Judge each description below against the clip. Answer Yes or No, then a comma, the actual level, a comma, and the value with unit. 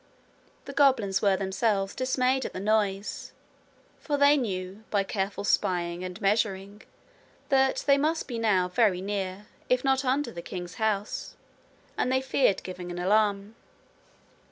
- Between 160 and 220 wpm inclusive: No, average, 145 wpm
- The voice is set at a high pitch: Yes, high, 205 Hz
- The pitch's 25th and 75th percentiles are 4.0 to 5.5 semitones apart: Yes, average, 5.1 semitones